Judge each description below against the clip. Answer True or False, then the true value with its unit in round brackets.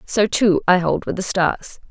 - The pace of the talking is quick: True (220 wpm)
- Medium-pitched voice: False (195 Hz)